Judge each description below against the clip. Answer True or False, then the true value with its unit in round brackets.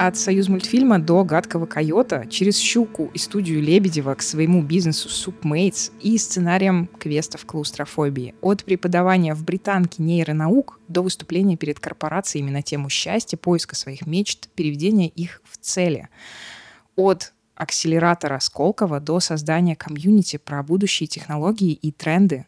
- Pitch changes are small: False (3.7 semitones)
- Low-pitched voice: False (170 Hz)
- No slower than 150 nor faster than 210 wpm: False (130 wpm)